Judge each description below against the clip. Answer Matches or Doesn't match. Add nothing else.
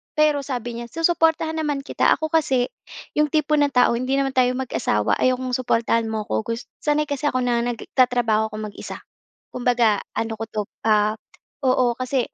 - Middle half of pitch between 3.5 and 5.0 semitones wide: Matches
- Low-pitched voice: Doesn't match